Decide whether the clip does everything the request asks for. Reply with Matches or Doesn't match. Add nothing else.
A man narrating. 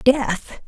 Doesn't match